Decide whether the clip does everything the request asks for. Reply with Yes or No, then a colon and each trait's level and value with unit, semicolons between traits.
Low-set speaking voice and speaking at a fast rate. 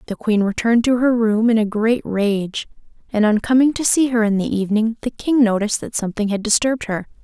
No: high, 225 Hz; fast, 225 wpm